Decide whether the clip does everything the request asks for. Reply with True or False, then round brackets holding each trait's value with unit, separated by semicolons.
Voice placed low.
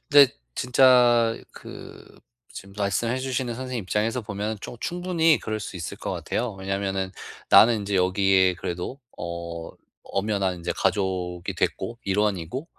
True (105 Hz)